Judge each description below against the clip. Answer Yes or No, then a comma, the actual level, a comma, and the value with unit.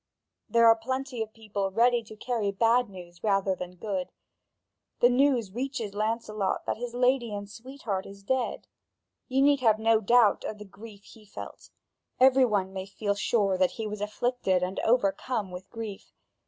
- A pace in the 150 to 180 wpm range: Yes, average, 170 wpm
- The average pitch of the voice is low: No, high, 215 Hz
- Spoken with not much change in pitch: No, average, 3.6 semitones